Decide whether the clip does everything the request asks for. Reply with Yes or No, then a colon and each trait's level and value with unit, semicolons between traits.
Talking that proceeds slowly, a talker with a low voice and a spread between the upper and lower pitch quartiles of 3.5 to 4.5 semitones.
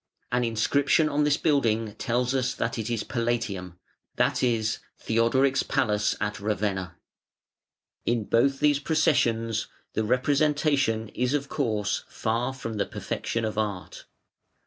Yes: slow, 130 wpm; low, 115 Hz; average, 3.9 semitones